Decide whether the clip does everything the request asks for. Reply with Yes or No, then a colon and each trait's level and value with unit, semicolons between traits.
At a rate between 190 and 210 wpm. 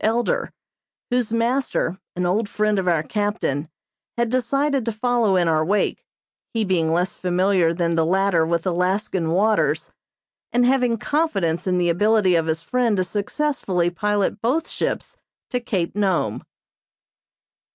No: average, 145 wpm